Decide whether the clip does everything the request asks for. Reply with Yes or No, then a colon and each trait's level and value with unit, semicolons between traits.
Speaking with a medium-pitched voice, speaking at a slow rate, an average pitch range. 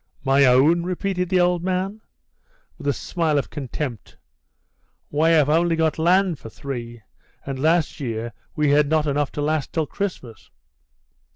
No: medium, 150 Hz; average, 160 wpm; average, 3.9 semitones